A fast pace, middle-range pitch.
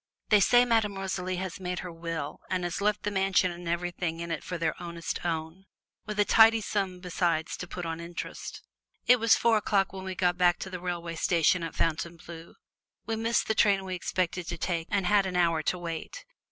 Yes: fast, 215 wpm; medium, 180 Hz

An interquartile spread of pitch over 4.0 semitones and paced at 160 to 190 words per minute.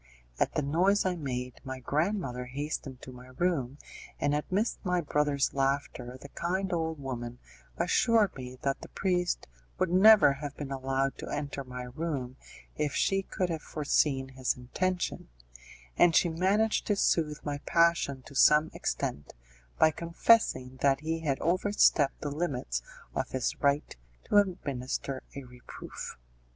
No: average, 4.8 semitones; average, 150 wpm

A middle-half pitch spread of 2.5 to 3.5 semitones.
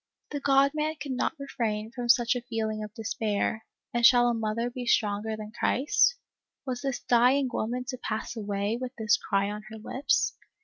Yes: average, 2.9 semitones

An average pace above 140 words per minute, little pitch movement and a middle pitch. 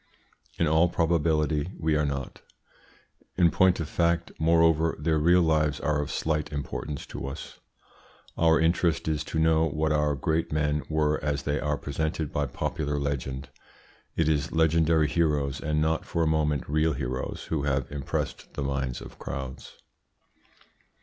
No: average, 155 wpm; narrow, 1.9 semitones; very low, 75 Hz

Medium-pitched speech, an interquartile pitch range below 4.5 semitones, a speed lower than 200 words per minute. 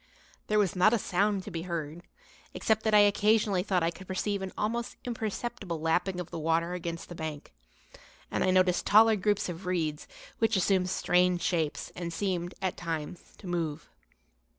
Yes: medium, 180 Hz; average, 3.4 semitones; average, 175 wpm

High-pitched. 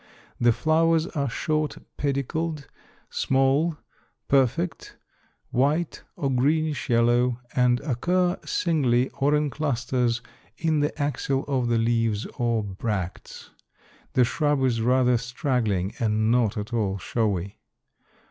No: low, 125 Hz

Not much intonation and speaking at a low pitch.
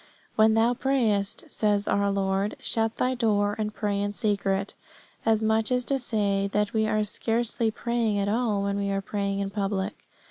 No: narrow, 2.0 semitones; high, 210 Hz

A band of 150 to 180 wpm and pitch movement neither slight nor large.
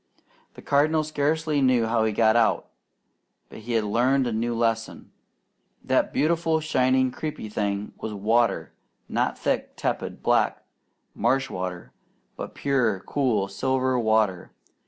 No: slow, 135 wpm; average, 4.0 semitones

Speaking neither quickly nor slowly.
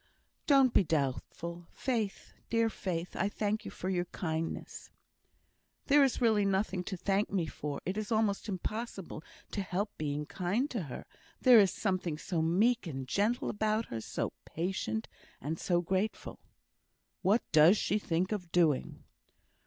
Yes: average, 155 wpm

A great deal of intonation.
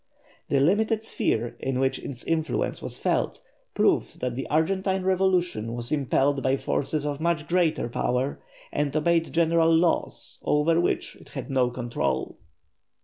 No: average, 4.4 semitones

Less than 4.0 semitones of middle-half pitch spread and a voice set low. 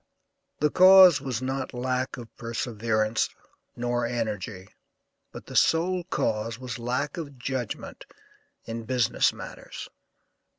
Yes: average, 3.0 semitones; low, 125 Hz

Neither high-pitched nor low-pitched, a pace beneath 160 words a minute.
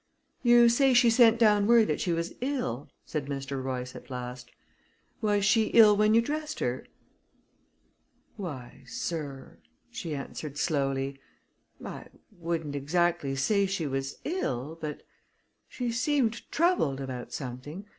Yes: medium, 170 Hz; slow, 135 wpm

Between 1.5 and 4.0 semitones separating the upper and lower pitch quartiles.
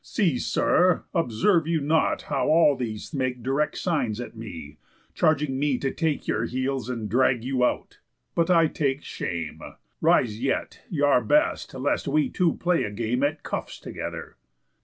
No: average, 4.4 semitones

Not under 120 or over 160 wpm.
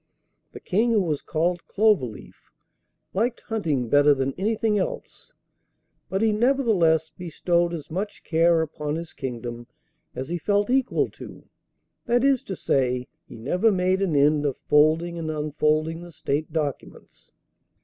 Yes: average, 145 wpm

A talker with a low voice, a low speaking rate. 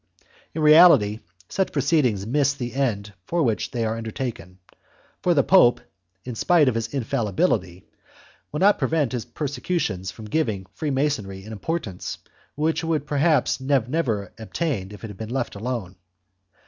No: low, 125 Hz; average, 155 wpm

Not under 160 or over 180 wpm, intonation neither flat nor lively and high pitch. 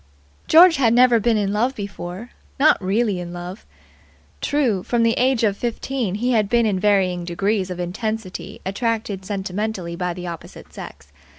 Yes: average, 165 wpm; average, 4.2 semitones; high, 205 Hz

